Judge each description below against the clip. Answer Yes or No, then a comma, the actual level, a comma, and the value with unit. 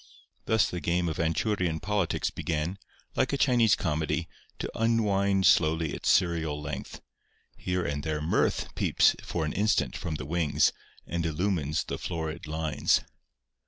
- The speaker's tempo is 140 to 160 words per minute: Yes, average, 145 wpm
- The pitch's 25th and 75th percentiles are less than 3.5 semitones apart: No, average, 3.8 semitones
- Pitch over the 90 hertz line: No, very low, 85 Hz